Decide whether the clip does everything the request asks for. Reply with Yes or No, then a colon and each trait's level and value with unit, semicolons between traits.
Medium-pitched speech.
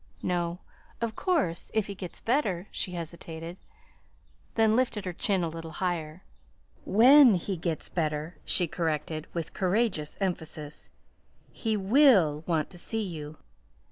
Yes: medium, 180 Hz